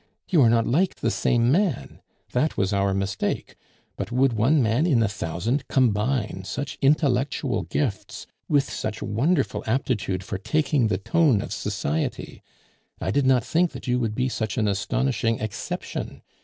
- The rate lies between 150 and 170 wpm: Yes, average, 160 wpm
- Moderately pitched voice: No, low, 120 Hz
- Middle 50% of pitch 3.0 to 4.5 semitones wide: No, average, 4.9 semitones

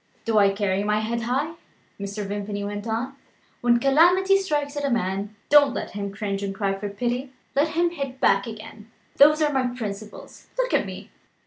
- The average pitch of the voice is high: Yes, high, 230 Hz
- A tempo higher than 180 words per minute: Yes, average, 190 wpm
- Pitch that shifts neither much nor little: No, wide, 5.8 semitones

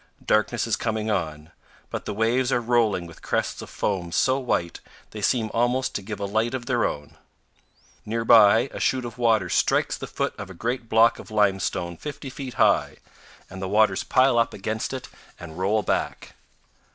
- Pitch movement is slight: No, average, 3.6 semitones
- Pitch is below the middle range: Yes, low, 110 Hz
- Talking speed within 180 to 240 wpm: Yes, average, 190 wpm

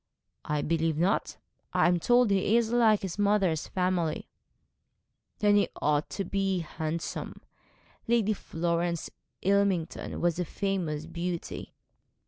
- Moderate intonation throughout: Yes, average, 3.3 semitones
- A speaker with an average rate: No, slow, 120 wpm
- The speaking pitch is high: No, medium, 180 Hz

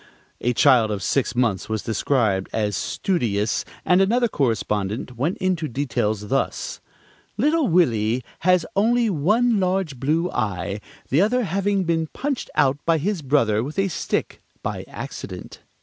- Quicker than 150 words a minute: No, average, 145 wpm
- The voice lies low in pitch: No, medium, 145 Hz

